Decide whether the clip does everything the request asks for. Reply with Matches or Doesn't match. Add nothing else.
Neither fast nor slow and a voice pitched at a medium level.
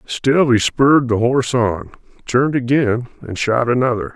Doesn't match